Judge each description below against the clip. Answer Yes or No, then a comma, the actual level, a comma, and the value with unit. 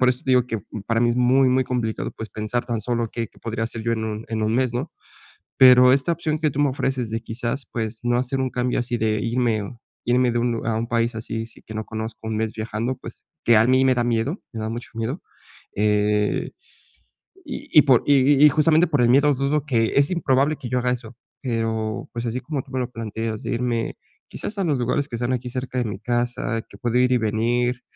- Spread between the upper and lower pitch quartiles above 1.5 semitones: Yes, narrow, 2.4 semitones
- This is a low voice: Yes, low, 120 Hz